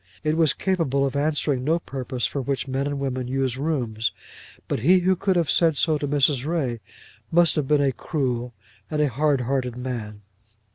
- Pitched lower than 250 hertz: Yes, medium, 140 Hz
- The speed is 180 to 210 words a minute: Yes, average, 185 wpm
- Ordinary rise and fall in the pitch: Yes, average, 3.4 semitones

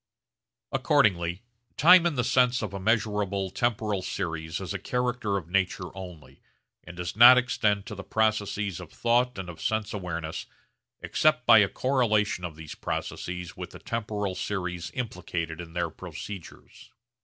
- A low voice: Yes, low, 100 Hz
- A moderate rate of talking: Yes, average, 155 wpm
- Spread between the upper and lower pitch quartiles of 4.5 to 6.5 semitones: No, average, 4.0 semitones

